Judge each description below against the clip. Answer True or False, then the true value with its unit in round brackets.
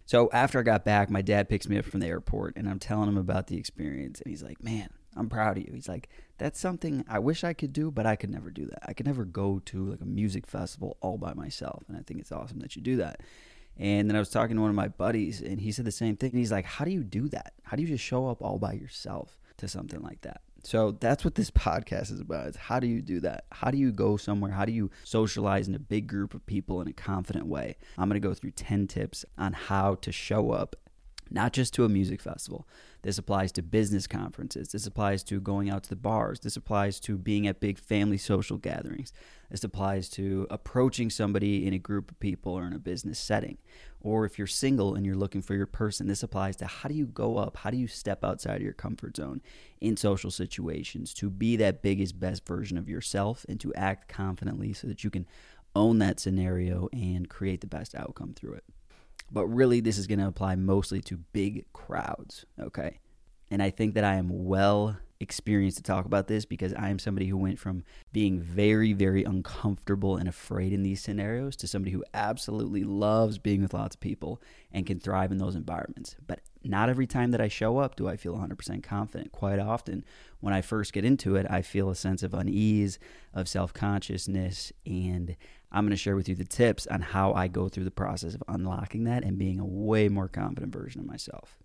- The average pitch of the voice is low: True (100 Hz)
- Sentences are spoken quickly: True (235 wpm)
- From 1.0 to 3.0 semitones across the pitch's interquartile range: True (2.4 semitones)